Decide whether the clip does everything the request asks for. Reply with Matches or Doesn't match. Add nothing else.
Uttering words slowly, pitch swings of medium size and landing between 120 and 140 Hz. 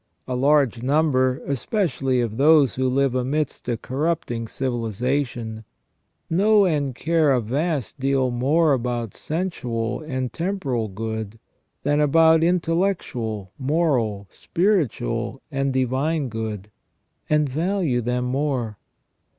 Matches